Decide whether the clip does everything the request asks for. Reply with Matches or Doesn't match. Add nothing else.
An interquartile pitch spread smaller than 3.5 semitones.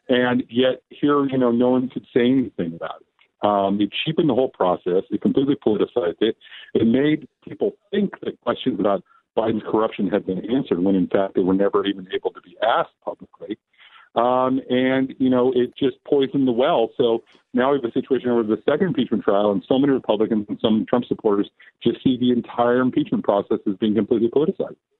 Doesn't match